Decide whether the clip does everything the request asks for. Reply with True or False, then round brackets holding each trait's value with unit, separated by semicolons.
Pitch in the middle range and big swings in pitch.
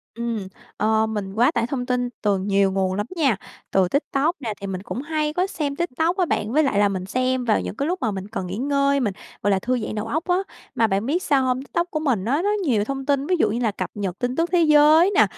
False (245 Hz; 6.1 semitones)